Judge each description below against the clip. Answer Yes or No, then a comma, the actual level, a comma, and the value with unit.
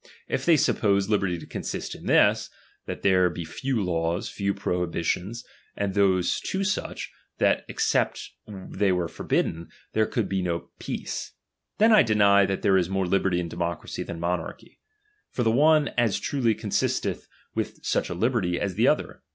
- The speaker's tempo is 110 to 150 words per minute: No, average, 165 wpm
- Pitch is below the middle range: Yes, very low, 95 Hz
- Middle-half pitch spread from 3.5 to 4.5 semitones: Yes, average, 4.1 semitones